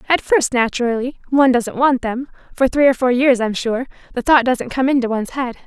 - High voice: Yes, very high, 255 Hz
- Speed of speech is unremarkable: No, fast, 210 wpm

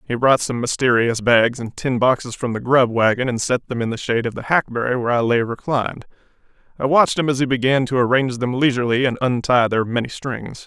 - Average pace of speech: No, fast, 225 wpm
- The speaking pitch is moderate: No, low, 125 Hz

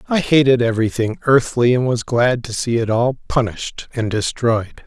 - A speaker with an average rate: Yes, average, 175 wpm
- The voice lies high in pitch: No, low, 120 Hz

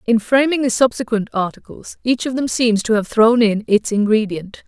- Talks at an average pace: Yes, average, 195 wpm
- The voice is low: No, high, 225 Hz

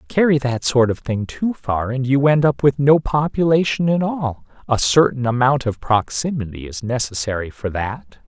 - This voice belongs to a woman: No, male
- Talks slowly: No, average, 180 wpm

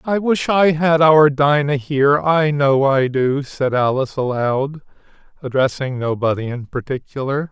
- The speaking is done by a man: Yes, male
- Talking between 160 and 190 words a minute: No, average, 145 wpm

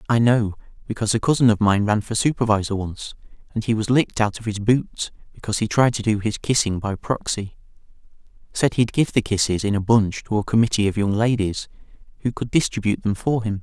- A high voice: No, low, 110 Hz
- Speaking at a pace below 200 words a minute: No, fast, 205 wpm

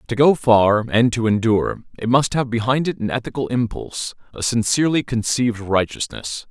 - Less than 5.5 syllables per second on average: Yes, 5.3 syllables/s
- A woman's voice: No, male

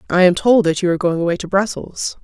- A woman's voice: Yes, female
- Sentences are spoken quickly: Yes, fast, 270 wpm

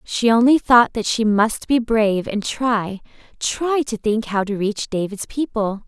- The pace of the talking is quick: No, average, 175 wpm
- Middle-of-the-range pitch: No, high, 225 Hz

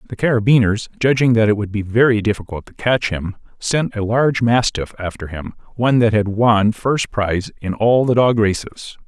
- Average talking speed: Yes, average, 190 wpm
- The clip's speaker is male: Yes, male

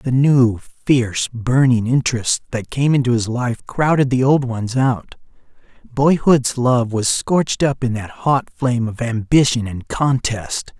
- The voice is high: No, low, 125 Hz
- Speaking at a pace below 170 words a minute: Yes, average, 155 wpm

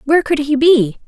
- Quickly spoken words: Yes, fast, 225 wpm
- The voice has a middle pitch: No, very high, 285 Hz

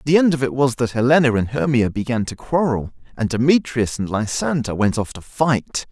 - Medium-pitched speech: No, low, 125 Hz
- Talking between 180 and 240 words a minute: Yes, fast, 205 wpm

